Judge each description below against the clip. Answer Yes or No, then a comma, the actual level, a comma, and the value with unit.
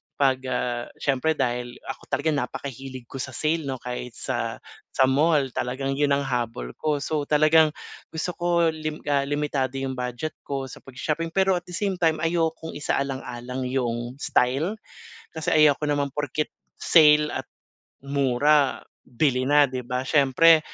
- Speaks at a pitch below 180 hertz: Yes, medium, 140 Hz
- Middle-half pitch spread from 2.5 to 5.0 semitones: Yes, average, 3.2 semitones